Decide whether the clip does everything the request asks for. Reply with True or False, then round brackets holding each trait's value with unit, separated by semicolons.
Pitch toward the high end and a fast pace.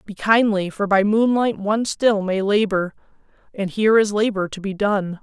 False (205 Hz; 185 wpm)